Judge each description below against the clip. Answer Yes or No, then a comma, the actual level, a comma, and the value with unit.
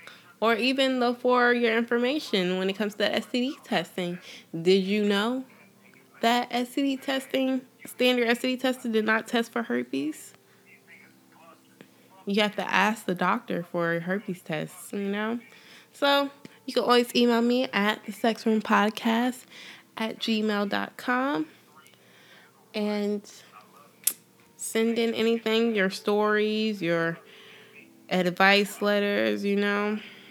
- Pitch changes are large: No, average, 3.4 semitones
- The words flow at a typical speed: No, slow, 120 wpm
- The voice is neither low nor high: No, high, 215 Hz